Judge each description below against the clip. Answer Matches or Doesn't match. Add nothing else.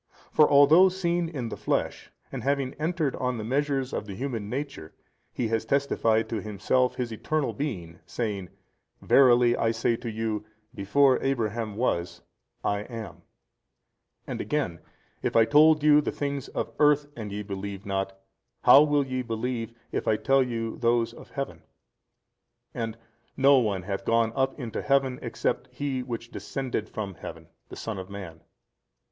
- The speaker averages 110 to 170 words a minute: Matches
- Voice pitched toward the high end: Doesn't match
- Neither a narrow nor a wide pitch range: Matches